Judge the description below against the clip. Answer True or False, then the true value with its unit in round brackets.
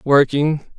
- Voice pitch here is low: False (145 Hz)